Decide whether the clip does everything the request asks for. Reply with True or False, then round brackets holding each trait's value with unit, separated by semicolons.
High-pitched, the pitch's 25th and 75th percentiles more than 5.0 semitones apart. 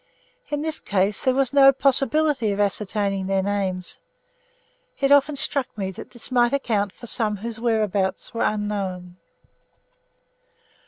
True (215 Hz; 5.4 semitones)